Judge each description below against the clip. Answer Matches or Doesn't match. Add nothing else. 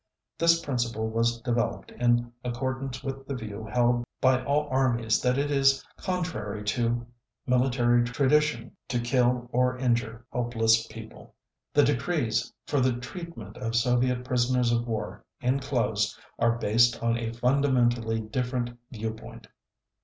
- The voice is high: Doesn't match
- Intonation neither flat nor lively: Doesn't match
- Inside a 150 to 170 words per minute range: Doesn't match